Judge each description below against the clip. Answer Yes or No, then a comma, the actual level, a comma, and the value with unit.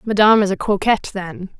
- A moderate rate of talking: Yes, average, 190 wpm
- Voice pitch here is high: Yes, high, 200 Hz